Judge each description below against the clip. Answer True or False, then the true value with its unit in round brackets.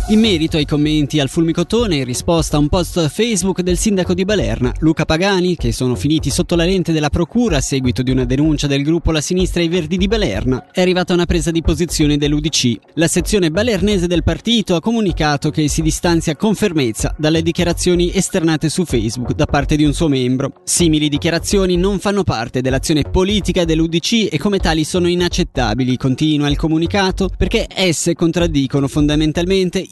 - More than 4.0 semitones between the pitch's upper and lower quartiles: False (3.7 semitones)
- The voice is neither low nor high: True (165 Hz)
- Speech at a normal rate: False (185 wpm)